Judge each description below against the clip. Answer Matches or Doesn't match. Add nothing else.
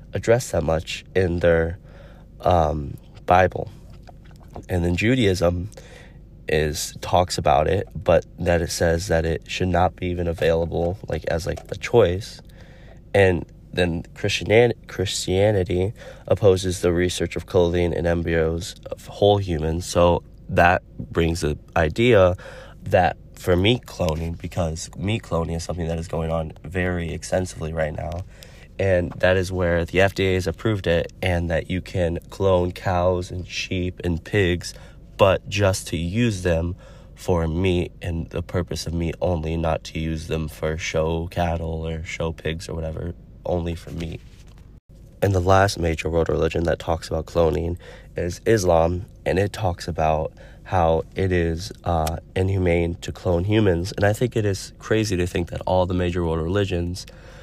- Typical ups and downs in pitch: Doesn't match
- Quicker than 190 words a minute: Doesn't match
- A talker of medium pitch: Doesn't match